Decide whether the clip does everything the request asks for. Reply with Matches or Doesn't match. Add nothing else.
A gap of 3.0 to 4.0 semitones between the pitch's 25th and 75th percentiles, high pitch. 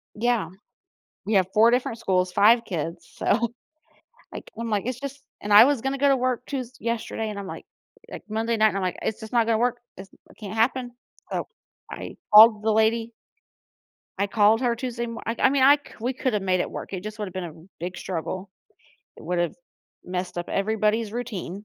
Matches